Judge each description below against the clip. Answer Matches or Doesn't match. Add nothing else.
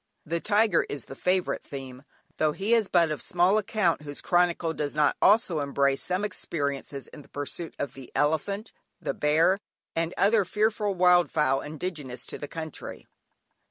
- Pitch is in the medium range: Matches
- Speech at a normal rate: Matches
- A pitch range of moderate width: Matches